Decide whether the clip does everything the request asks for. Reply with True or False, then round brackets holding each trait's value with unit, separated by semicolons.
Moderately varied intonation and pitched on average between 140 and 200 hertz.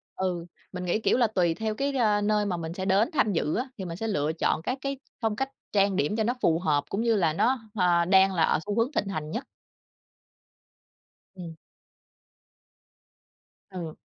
True (4.5 semitones; 195 Hz)